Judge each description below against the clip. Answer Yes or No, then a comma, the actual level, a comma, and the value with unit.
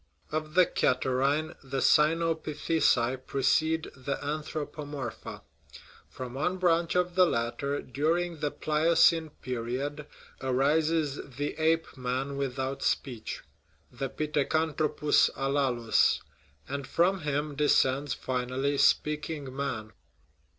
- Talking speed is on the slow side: Yes, slow, 105 wpm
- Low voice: No, medium, 145 Hz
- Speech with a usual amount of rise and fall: Yes, average, 3.0 semitones